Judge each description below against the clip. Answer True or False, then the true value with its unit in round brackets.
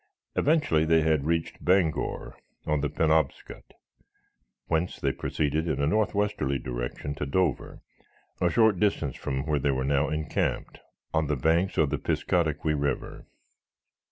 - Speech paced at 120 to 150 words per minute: True (140 wpm)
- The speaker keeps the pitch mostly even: False (3.0 semitones)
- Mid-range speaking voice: False (80 Hz)